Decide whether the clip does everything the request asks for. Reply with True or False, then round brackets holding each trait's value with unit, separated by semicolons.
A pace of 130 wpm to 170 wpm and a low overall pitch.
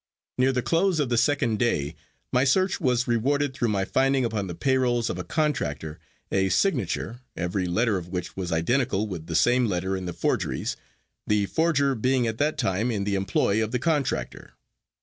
False (190 wpm; 115 Hz)